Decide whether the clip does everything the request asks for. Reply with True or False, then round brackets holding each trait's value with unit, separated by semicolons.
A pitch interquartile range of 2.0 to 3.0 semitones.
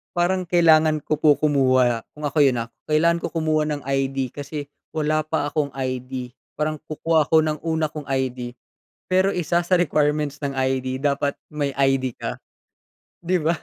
True (2.7 semitones)